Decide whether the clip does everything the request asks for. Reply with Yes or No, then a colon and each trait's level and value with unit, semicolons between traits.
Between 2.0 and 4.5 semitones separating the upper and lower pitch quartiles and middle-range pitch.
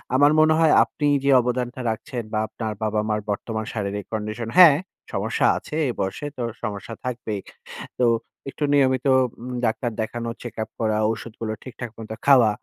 No: average, 2.8 semitones; low, 115 Hz